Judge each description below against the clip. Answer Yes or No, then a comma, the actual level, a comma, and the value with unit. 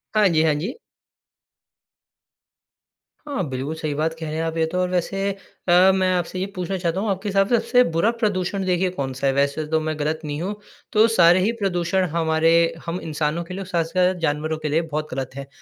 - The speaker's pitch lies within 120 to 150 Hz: No, medium, 170 Hz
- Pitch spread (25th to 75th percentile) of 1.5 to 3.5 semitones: Yes, average, 3.2 semitones